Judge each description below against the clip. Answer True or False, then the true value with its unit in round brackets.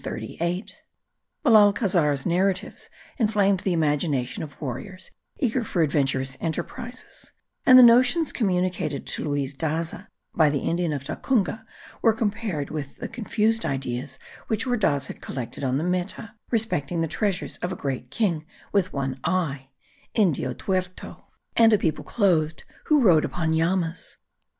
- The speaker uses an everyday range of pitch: False (6.5 semitones)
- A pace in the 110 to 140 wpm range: True (135 wpm)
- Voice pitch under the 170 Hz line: False (175 Hz)